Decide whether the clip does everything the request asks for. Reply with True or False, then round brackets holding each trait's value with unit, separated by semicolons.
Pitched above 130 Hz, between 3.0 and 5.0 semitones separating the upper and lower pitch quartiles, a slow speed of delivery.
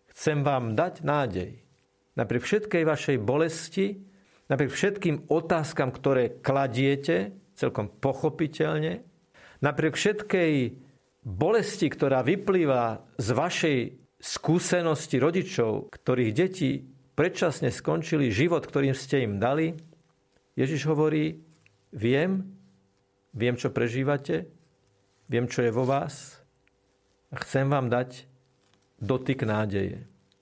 True (140 Hz; 4.6 semitones; 100 wpm)